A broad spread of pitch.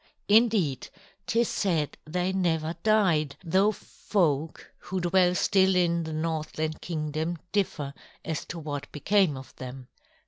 No: average, 3.7 semitones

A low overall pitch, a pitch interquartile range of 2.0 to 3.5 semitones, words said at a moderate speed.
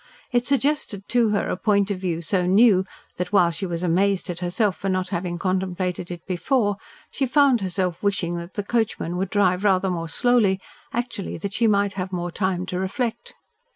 No: high, 190 Hz; average, 2.7 semitones; average, 190 wpm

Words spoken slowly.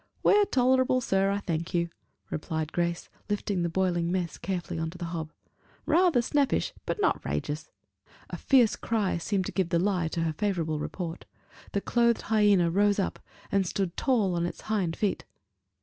No: average, 175 wpm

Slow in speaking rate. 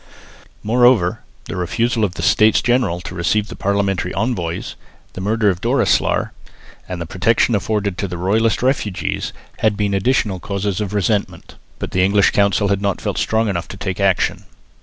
No: average, 165 wpm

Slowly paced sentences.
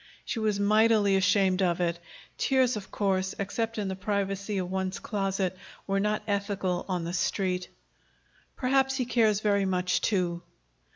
No: average, 155 wpm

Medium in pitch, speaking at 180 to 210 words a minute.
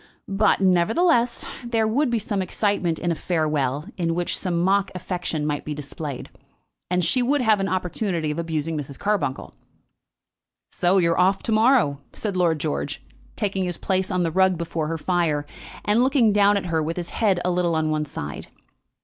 Yes: medium, 180 Hz; average, 185 wpm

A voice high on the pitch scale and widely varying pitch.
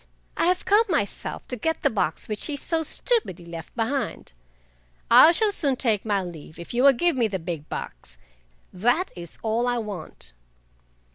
Yes: high, 225 Hz; wide, 8.9 semitones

